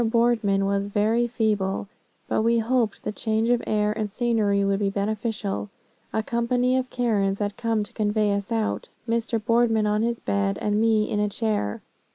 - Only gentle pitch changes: Yes, narrow, 2.3 semitones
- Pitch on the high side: Yes, high, 215 Hz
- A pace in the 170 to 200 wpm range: Yes, average, 180 wpm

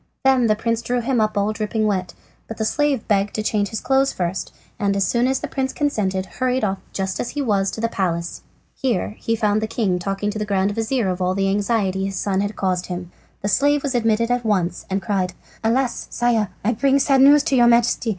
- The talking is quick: Yes, fast, 235 wpm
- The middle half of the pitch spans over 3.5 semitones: Yes, average, 3.9 semitones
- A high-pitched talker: Yes, high, 215 Hz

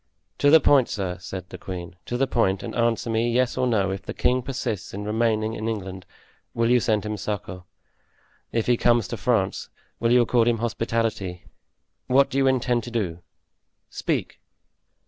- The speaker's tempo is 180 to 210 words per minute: Yes, average, 185 wpm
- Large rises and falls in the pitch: No, average, 3.7 semitones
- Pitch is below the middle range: Yes, low, 115 Hz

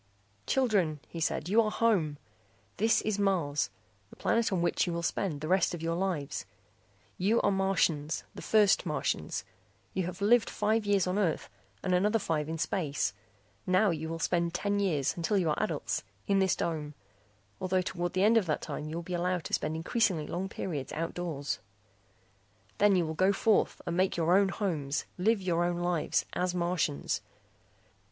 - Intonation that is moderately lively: Yes, average, 3.4 semitones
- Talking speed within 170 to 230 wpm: Yes, average, 180 wpm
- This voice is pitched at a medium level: Yes, medium, 180 Hz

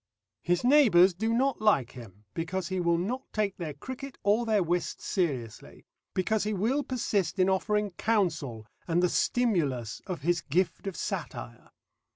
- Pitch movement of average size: Yes, average, 4.6 semitones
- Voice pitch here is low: No, medium, 185 Hz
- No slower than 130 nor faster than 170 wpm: Yes, average, 160 wpm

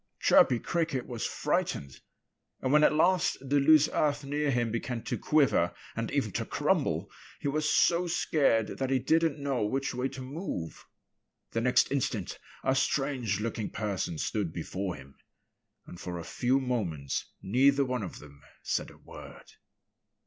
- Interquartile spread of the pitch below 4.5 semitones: No, wide, 5.4 semitones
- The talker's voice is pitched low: Yes, low, 130 Hz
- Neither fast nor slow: Yes, average, 160 wpm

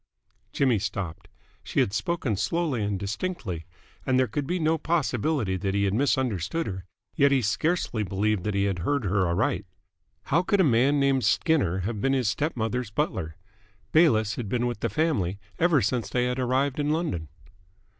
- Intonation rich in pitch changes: Yes, wide, 6.4 semitones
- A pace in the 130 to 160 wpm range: No, average, 180 wpm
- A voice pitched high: No, low, 120 Hz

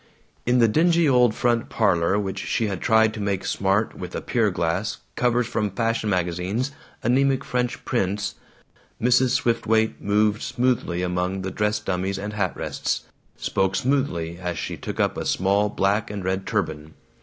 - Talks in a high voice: No, low, 105 Hz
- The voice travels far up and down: No, average, 4.1 semitones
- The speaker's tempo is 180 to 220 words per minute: No, average, 165 wpm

